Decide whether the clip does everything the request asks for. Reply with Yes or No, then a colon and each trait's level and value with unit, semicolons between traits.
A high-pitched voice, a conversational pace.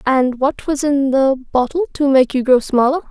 No: very high, 270 Hz; fast, 215 wpm